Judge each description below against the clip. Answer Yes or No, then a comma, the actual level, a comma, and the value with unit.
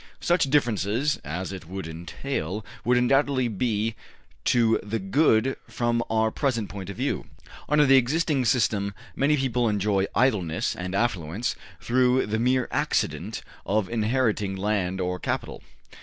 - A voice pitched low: Yes, low, 110 Hz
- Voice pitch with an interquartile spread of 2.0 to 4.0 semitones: No, average, 4.7 semitones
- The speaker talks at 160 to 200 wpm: No, average, 140 wpm